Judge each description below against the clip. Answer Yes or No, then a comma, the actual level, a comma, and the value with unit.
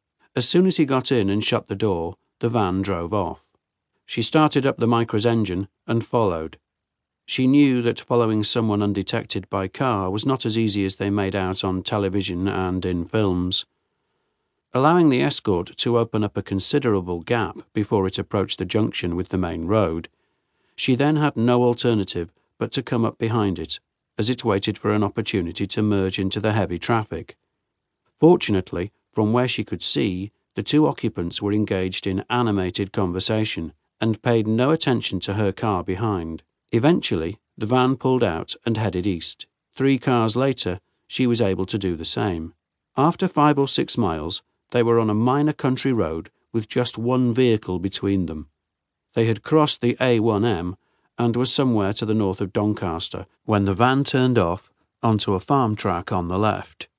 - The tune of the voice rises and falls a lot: No, average, 4.1 semitones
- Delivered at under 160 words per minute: No, average, 175 wpm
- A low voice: Yes, low, 105 Hz